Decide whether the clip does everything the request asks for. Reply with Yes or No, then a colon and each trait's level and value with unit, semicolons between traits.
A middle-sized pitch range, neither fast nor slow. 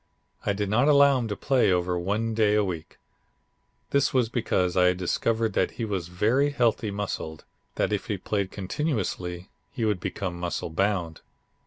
Yes: average, 4.1 semitones; average, 175 wpm